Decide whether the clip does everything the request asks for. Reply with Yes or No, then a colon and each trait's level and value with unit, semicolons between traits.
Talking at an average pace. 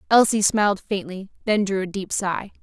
Yes: average, 185 wpm